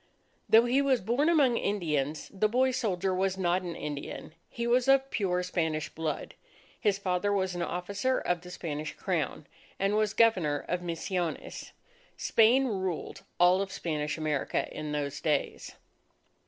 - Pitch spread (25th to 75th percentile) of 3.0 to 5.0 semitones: No, wide, 5.4 semitones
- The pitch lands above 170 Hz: Yes, medium, 185 Hz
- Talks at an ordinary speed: Yes, average, 150 wpm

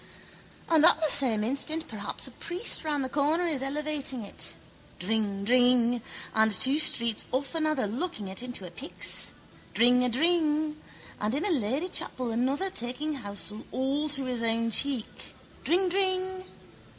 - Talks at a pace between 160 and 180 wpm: No, average, 140 wpm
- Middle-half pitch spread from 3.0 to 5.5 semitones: Yes, average, 5.1 semitones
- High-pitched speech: Yes, very high, 265 Hz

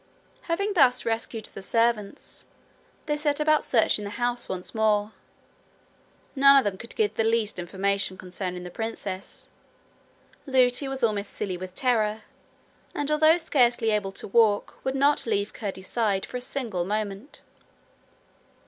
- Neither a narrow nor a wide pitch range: Yes, average, 4.9 semitones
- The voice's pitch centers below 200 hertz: No, high, 225 Hz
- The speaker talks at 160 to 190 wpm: No, average, 145 wpm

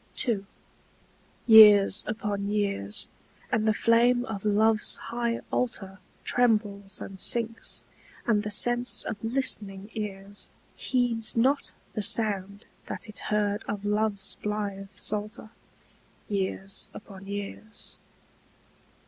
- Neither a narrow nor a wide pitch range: No, narrow, 2.1 semitones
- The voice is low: No, high, 210 Hz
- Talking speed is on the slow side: Yes, slow, 105 wpm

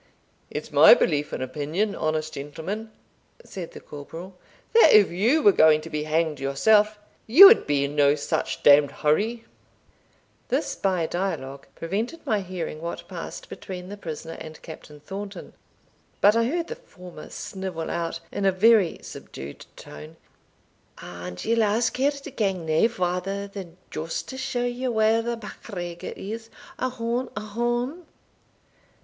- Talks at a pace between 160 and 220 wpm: No, average, 150 wpm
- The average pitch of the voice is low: No, high, 190 Hz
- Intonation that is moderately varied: No, wide, 6.3 semitones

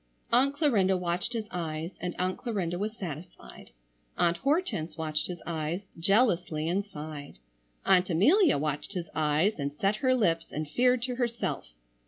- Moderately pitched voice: Yes, medium, 180 Hz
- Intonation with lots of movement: Yes, wide, 6.2 semitones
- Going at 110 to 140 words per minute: No, average, 155 wpm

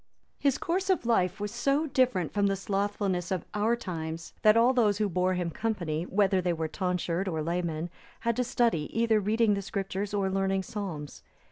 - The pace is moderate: Yes, average, 190 wpm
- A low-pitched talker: No, high, 195 Hz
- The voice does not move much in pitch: No, average, 3.9 semitones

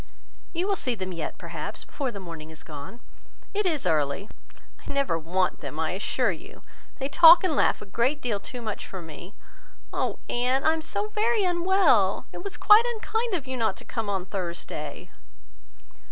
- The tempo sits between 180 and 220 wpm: Yes, average, 185 wpm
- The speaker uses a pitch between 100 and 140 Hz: No, high, 235 Hz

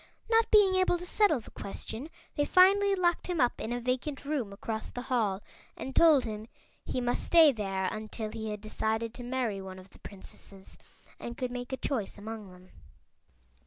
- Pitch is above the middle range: Yes, high, 245 Hz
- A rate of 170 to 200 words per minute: Yes, average, 190 wpm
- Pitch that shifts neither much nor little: No, wide, 6.0 semitones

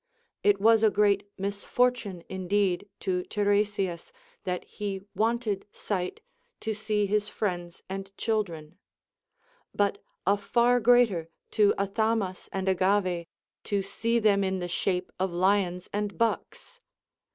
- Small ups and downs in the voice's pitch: Yes, narrow, 2.3 semitones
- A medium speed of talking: No, slow, 125 wpm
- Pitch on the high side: Yes, high, 200 Hz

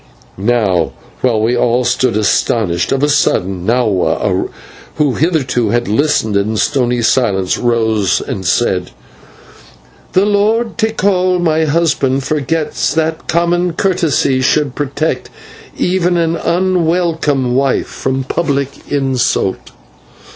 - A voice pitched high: No, low, 135 Hz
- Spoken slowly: Yes, slow, 110 wpm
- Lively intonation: Yes, wide, 6.3 semitones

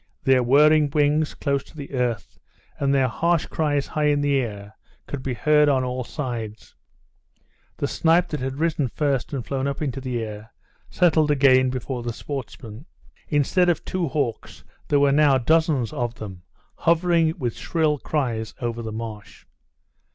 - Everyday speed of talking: Yes, average, 165 wpm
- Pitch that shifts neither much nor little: Yes, average, 3.9 semitones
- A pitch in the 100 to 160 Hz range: Yes, medium, 140 Hz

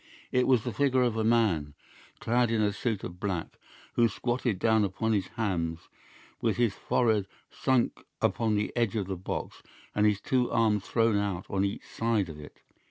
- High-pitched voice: No, low, 110 Hz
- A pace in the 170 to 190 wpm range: Yes, average, 185 wpm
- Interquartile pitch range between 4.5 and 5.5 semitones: No, average, 3.3 semitones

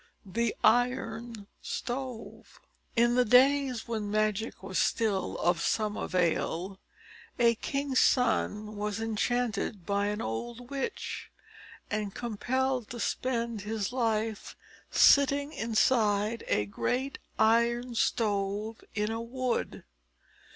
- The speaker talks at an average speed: No, slow, 110 wpm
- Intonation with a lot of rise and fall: No, average, 2.9 semitones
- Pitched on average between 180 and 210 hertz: No, high, 225 Hz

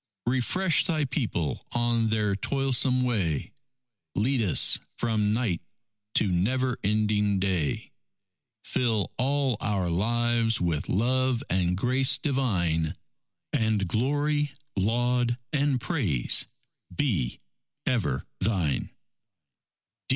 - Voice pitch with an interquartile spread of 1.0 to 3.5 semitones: No, average, 5.0 semitones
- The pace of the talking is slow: Yes, slow, 95 wpm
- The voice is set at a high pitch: No, low, 115 Hz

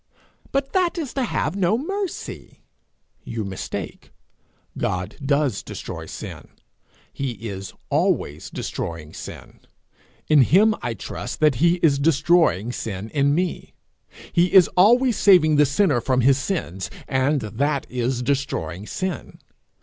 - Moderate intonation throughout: No, wide, 7.6 semitones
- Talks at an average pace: No, slow, 130 wpm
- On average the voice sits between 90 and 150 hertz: Yes, medium, 140 Hz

